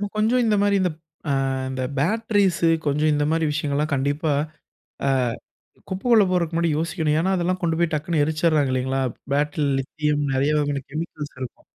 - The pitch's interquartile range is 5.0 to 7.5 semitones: No, average, 3.3 semitones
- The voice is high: No, medium, 155 Hz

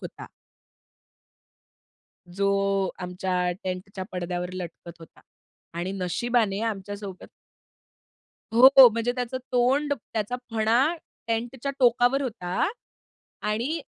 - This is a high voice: Yes, high, 215 Hz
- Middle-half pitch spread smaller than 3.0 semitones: No, average, 4.7 semitones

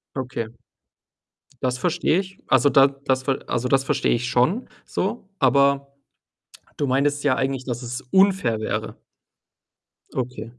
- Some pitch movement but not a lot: No, narrow, 2.3 semitones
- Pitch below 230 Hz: Yes, low, 135 Hz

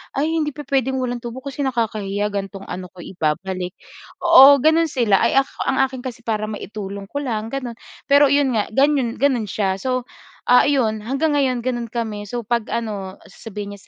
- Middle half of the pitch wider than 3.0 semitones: Yes, average, 4.6 semitones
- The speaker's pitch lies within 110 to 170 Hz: No, high, 235 Hz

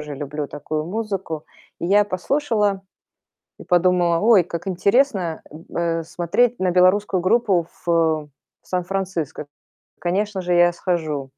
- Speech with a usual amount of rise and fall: Yes, average, 3.1 semitones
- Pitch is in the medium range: Yes, medium, 180 Hz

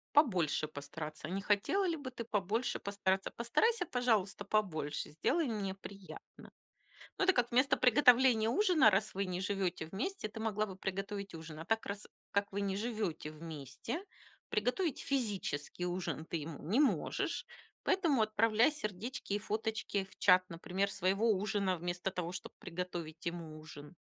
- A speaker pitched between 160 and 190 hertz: No, high, 200 Hz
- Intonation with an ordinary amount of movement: Yes, average, 4.6 semitones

